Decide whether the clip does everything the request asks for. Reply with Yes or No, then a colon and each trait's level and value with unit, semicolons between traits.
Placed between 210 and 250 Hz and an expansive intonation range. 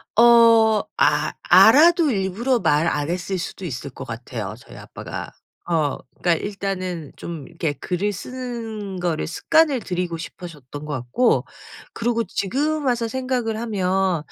No: high, 195 Hz; wide, 5.7 semitones